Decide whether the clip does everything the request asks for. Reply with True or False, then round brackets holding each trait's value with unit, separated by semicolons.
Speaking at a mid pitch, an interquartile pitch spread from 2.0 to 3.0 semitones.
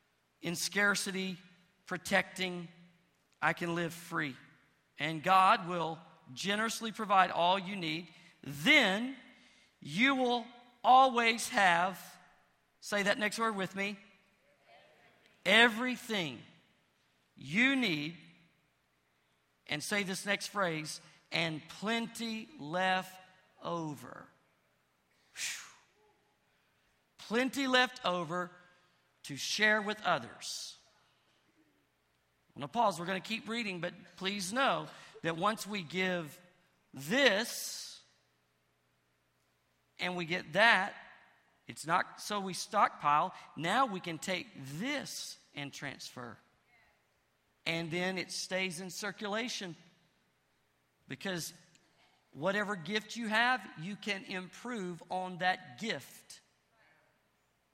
False (180 Hz; 5.0 semitones)